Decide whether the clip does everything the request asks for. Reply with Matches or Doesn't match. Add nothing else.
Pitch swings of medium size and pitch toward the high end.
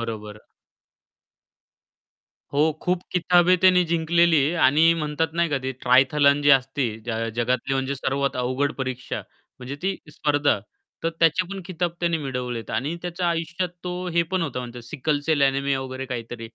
Doesn't match